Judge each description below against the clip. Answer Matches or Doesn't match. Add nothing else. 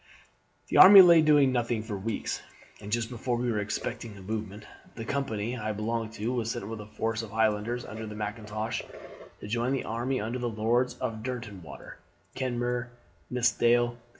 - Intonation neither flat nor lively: Doesn't match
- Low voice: Matches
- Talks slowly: Doesn't match